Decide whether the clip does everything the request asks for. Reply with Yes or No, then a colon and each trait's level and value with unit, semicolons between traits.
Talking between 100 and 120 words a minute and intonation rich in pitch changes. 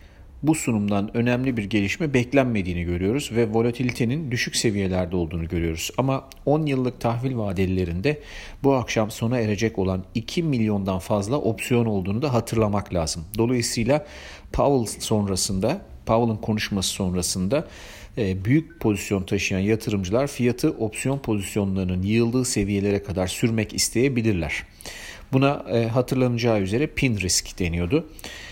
No: average, 115 wpm; average, 4.5 semitones